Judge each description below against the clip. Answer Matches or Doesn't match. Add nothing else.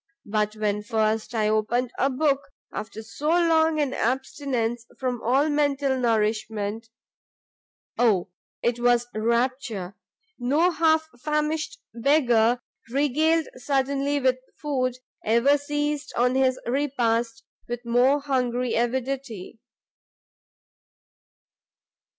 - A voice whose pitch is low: Doesn't match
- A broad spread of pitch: Doesn't match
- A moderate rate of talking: Doesn't match